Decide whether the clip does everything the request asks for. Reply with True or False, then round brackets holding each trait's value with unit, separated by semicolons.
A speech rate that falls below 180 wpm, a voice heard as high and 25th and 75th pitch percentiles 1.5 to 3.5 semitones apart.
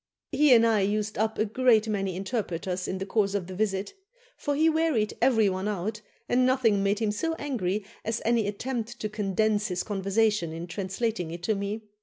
False (195 wpm; 210 Hz; 2.9 semitones)